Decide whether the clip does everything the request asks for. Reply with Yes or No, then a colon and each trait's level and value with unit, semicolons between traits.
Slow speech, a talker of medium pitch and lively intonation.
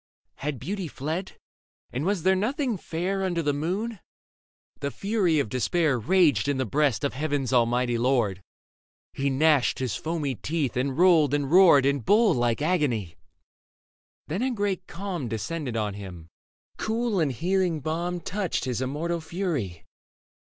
No: average, 150 wpm; medium, 150 Hz; wide, 6.1 semitones